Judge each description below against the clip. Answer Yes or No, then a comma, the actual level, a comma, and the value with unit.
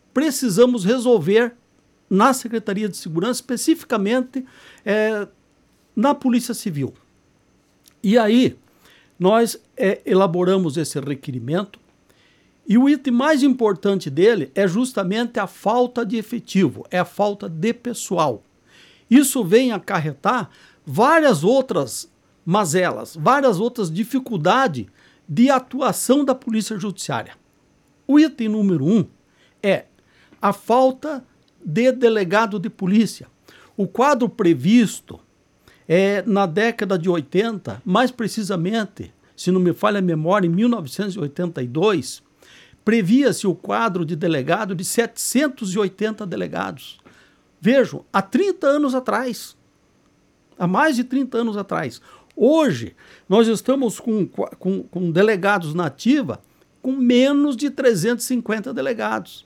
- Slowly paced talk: Yes, slow, 110 wpm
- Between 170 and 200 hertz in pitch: No, high, 215 Hz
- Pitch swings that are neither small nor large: Yes, average, 4.8 semitones